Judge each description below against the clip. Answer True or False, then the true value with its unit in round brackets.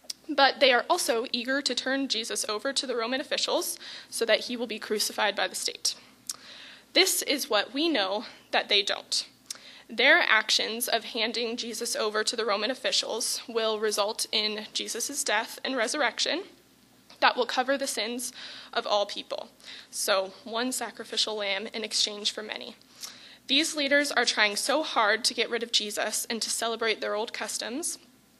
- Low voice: False (235 Hz)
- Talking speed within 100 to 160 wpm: False (170 wpm)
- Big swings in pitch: False (3.9 semitones)